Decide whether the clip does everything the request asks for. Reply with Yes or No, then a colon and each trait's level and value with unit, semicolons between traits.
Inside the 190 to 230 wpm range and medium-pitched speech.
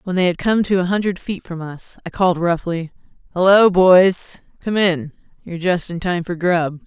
Yes: average, 200 wpm; medium, 180 Hz